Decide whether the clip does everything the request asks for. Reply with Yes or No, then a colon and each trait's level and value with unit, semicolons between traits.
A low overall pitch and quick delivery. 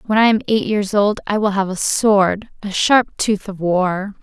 No: high, 200 Hz; fast, 225 wpm